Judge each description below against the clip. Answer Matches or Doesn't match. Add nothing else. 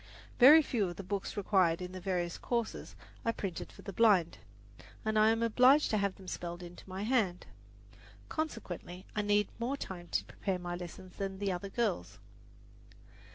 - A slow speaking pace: Doesn't match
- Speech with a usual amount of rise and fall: Matches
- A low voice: Doesn't match